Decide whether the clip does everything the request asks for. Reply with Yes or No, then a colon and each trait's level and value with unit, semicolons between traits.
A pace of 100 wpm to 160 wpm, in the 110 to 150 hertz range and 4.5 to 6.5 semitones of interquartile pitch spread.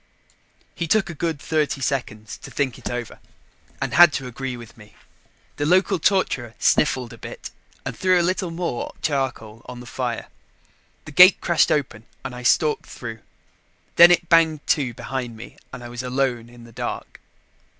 No: average, 175 wpm; low, 135 Hz; wide, 5.5 semitones